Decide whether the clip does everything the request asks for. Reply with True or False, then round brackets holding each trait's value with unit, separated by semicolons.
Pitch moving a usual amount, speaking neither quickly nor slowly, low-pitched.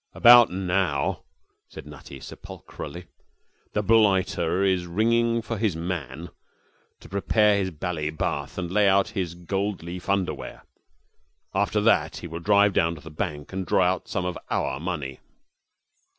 True (3.3 semitones; 145 wpm; 90 Hz)